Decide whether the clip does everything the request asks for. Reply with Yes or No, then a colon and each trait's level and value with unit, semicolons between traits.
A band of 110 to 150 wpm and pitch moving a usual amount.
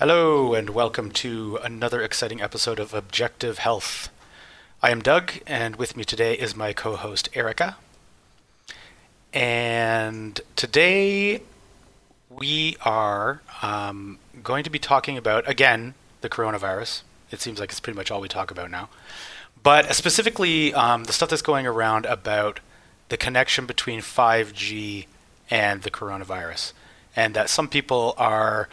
Yes: average, 140 wpm; average, 4.7 semitones